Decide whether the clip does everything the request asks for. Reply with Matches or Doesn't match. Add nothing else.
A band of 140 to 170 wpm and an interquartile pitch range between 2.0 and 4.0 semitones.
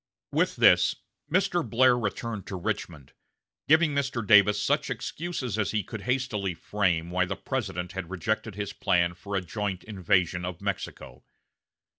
Doesn't match